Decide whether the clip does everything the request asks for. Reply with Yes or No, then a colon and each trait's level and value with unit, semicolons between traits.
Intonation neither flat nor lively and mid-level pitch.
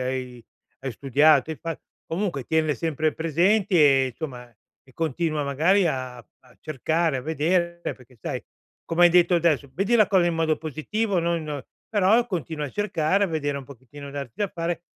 Yes: average, 3.7 semitones; medium, 155 Hz